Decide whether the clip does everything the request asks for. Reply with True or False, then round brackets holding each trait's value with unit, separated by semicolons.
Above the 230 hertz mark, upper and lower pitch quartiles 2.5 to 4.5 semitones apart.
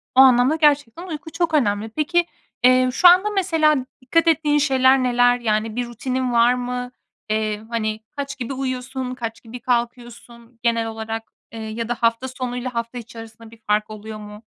True (245 Hz; 2.8 semitones)